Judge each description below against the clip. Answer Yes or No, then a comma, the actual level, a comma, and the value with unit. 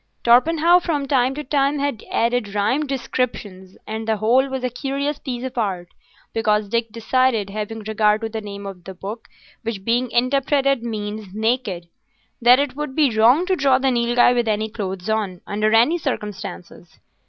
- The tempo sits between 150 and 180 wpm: Yes, average, 175 wpm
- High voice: Yes, high, 235 Hz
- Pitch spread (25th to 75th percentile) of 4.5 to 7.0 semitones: No, average, 3.9 semitones